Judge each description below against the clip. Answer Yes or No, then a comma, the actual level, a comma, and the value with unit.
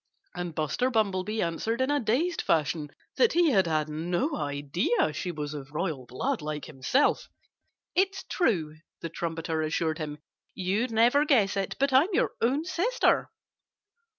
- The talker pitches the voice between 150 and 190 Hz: Yes, medium, 185 Hz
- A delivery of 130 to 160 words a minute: Yes, average, 150 wpm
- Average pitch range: No, wide, 9.0 semitones